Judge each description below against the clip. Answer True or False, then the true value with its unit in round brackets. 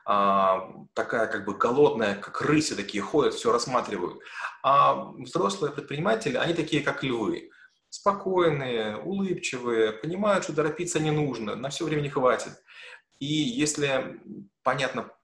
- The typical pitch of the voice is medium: True (150 Hz)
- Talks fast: False (125 wpm)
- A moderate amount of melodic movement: False (6.0 semitones)